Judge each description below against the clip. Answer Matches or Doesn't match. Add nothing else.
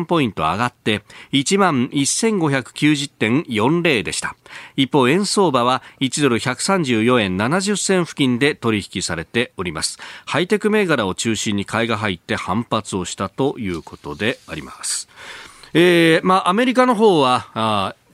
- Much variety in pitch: Matches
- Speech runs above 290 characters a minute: Doesn't match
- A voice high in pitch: Doesn't match